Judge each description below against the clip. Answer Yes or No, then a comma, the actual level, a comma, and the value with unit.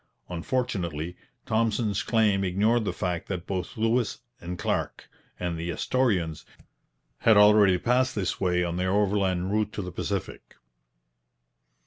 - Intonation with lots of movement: No, average, 3.6 semitones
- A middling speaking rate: No, slow, 130 wpm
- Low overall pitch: Yes, very low, 95 Hz